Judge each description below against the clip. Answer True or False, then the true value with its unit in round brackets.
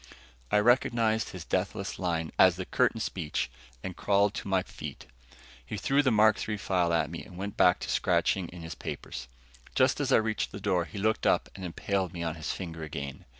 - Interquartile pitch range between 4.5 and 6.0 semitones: False (3.8 semitones)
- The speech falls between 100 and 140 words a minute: False (205 wpm)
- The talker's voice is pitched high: False (95 Hz)